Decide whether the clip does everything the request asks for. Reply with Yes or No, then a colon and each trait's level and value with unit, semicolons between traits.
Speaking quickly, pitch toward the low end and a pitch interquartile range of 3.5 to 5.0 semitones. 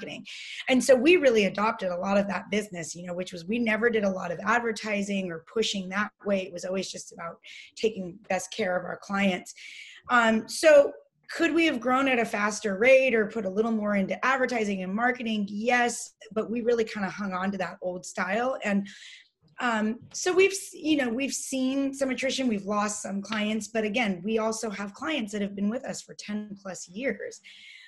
No: fast, 210 wpm; high, 215 Hz; average, 4.2 semitones